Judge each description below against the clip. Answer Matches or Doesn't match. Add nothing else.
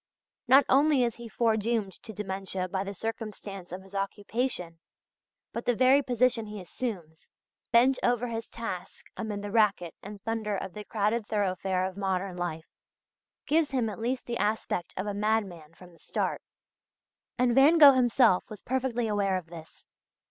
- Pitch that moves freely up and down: Doesn't match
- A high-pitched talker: Matches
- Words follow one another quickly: Doesn't match